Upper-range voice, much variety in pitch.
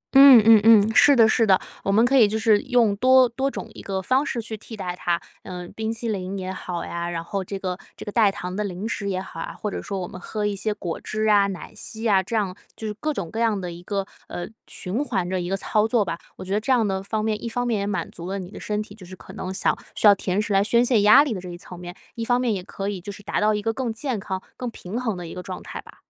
No: high, 205 Hz; average, 3.2 semitones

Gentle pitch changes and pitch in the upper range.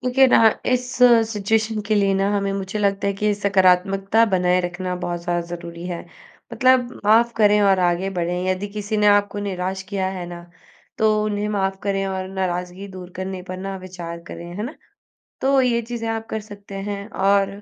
Yes: narrow, 2.3 semitones; high, 195 Hz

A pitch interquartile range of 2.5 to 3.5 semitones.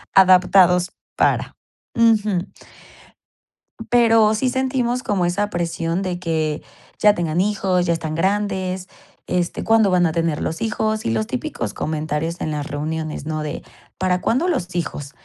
No: average, 4.4 semitones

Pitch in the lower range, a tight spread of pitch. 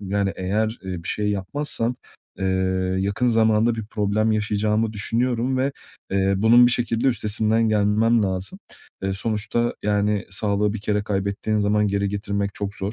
Yes: low, 105 Hz; narrow, 2.0 semitones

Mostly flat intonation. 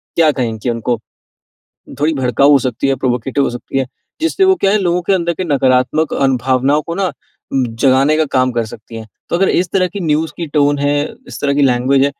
No: average, 4.0 semitones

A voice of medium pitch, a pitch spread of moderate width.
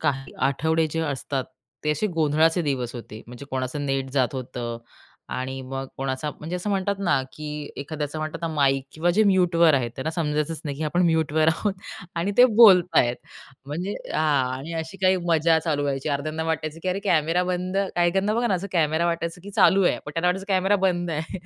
Yes: medium, 160 Hz; average, 4.0 semitones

